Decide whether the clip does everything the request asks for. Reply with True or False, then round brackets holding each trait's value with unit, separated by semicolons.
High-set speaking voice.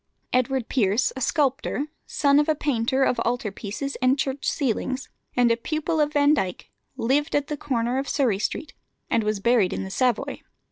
True (260 Hz)